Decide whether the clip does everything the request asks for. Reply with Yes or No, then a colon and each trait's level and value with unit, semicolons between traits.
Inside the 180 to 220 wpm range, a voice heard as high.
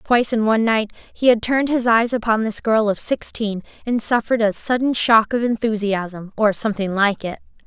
Yes: average, 195 wpm; high, 220 Hz